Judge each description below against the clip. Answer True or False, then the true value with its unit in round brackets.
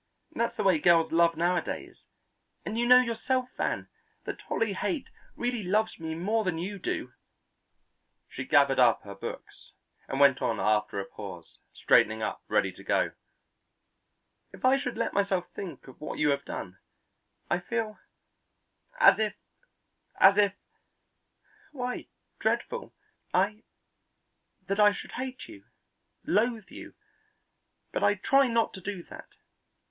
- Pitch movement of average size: False (7.1 semitones)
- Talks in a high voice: True (195 Hz)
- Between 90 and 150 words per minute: True (145 wpm)